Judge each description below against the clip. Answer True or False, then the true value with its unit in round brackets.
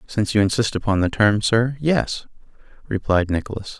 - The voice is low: True (110 Hz)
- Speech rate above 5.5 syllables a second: False (5.3 syllables/s)